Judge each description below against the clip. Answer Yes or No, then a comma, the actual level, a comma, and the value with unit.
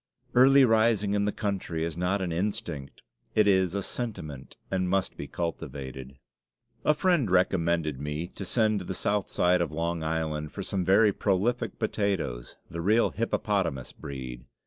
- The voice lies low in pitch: Yes, very low, 95 Hz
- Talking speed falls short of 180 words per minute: Yes, average, 160 wpm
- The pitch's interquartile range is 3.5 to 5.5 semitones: Yes, average, 4.7 semitones